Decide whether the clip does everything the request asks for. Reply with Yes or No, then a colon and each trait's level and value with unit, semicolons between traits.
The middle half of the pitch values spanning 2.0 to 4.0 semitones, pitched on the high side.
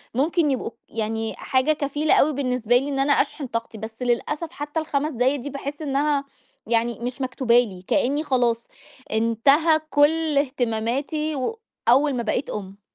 Yes: average, 3.7 semitones; very high, 270 Hz